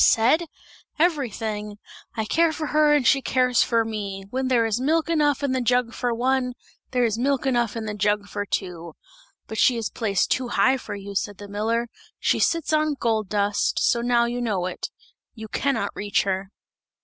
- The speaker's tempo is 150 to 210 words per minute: Yes, average, 195 wpm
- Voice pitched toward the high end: Yes, high, 235 Hz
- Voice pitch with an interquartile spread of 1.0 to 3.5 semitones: No, average, 4.1 semitones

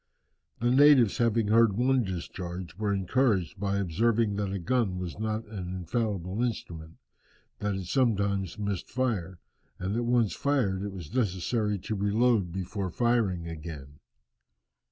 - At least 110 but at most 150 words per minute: Yes, average, 140 wpm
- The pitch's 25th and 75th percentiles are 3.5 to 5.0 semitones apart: Yes, average, 4.1 semitones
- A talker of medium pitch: No, low, 100 Hz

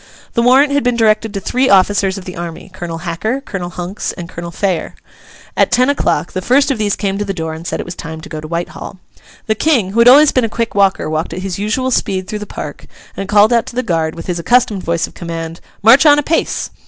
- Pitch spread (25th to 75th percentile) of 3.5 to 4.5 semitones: No, wide, 5.4 semitones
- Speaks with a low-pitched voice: No, high, 195 Hz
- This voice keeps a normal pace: No, fast, 250 wpm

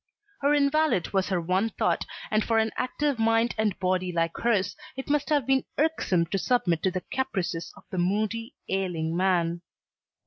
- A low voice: No, high, 205 Hz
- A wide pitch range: Yes, wide, 5.8 semitones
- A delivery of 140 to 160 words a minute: No, average, 175 wpm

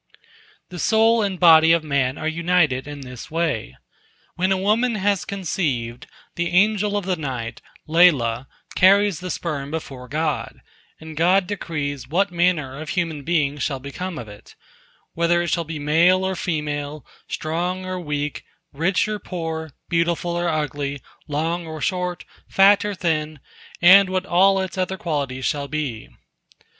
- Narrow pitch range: No, average, 4.0 semitones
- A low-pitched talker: No, medium, 165 Hz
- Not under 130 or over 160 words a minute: Yes, average, 150 wpm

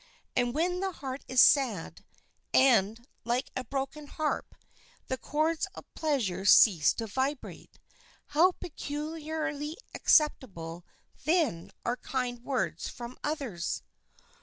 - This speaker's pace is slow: Yes, slow, 110 wpm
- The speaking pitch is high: Yes, very high, 270 Hz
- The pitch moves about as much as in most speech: Yes, average, 4.4 semitones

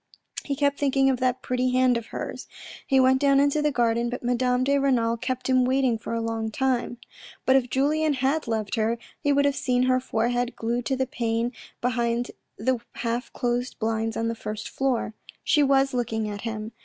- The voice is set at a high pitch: Yes, very high, 250 Hz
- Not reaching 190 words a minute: No, average, 200 wpm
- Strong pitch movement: No, narrow, 2.5 semitones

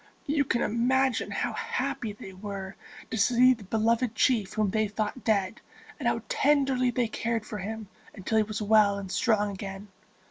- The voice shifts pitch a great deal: No, average, 3.6 semitones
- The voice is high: Yes, high, 220 Hz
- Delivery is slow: No, average, 175 wpm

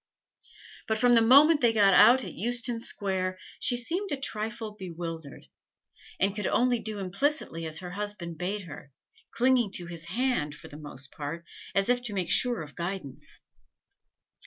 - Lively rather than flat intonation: Yes, wide, 6.0 semitones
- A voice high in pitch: Yes, high, 205 Hz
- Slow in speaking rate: No, average, 170 wpm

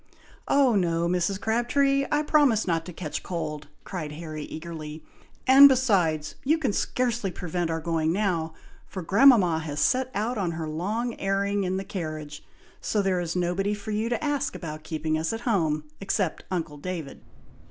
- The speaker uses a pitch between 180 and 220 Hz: Yes, medium, 185 Hz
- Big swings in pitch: Yes, wide, 5.8 semitones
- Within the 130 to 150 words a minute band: No, average, 170 wpm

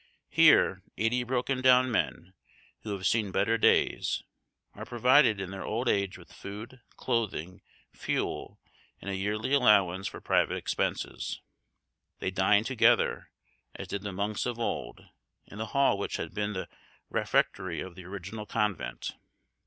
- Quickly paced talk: No, average, 145 wpm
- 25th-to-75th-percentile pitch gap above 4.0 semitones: No, average, 3.7 semitones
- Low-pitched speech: Yes, low, 105 Hz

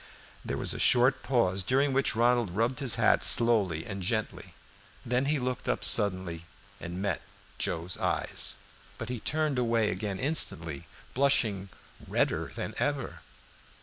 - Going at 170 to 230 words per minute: No, average, 145 wpm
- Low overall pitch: Yes, low, 115 Hz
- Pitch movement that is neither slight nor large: Yes, average, 4.9 semitones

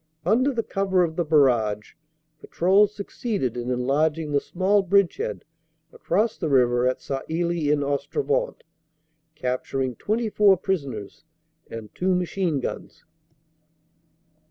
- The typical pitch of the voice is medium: Yes, medium, 165 Hz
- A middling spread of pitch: No, wide, 6.8 semitones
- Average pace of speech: No, slow, 110 wpm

